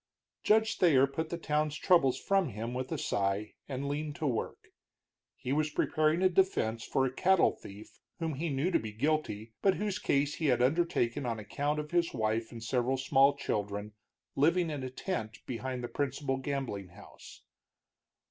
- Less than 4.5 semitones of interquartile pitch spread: No, average, 5.0 semitones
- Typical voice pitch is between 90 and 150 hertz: Yes, medium, 140 Hz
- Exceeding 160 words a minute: Yes, average, 180 wpm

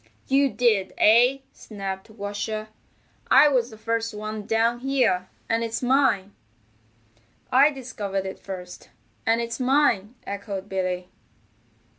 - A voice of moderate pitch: No, high, 220 Hz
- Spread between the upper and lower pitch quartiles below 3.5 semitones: No, average, 3.9 semitones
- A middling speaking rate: No, slow, 120 wpm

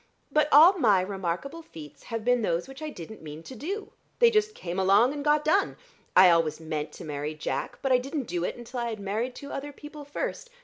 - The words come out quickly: Yes, fast, 225 wpm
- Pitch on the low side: No, high, 240 Hz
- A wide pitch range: Yes, wide, 9.0 semitones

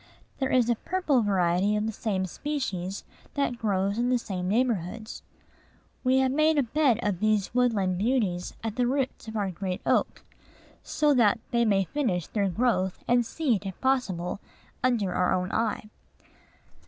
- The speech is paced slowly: No, average, 165 wpm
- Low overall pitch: No, high, 220 Hz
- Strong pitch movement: No, average, 4.9 semitones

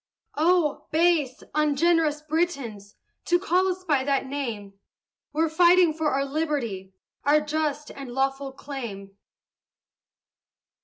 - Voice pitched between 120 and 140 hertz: No, very high, 295 Hz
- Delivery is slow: Yes, slow, 110 wpm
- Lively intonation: No, average, 3.4 semitones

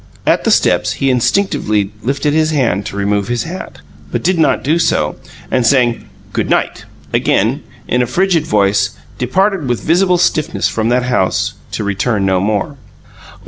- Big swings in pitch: Yes, wide, 7.4 semitones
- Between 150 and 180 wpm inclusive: Yes, average, 160 wpm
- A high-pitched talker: No, low, 125 Hz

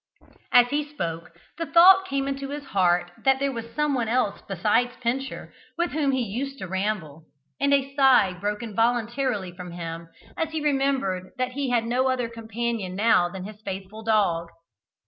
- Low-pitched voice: No, high, 235 Hz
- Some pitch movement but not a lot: No, wide, 6.1 semitones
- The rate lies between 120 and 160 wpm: No, average, 170 wpm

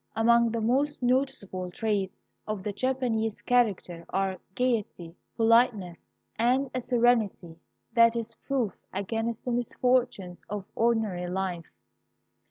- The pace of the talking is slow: Yes, slow, 115 wpm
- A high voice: Yes, high, 225 Hz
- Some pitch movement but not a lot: Yes, average, 4.2 semitones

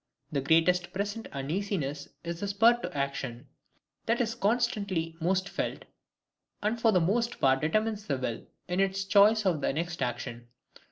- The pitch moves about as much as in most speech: No, wide, 6.1 semitones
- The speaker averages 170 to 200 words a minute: No, average, 160 wpm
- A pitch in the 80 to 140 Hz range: No, medium, 185 Hz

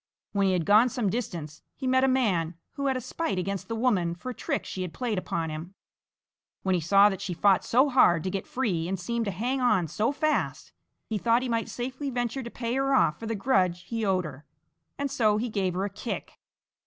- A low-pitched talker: No, high, 210 Hz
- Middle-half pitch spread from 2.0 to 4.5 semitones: No, average, 5.3 semitones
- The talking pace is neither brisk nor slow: No, fast, 235 wpm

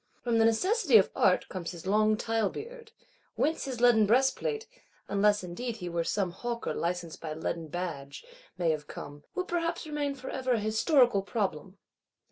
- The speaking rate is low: No, average, 165 wpm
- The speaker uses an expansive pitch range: Yes, wide, 6.8 semitones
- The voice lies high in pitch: Yes, high, 215 Hz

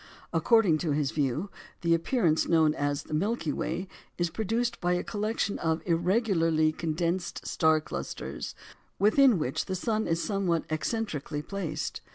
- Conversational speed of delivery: Yes, average, 145 wpm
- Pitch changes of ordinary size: Yes, average, 4.6 semitones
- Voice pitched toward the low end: No, medium, 170 Hz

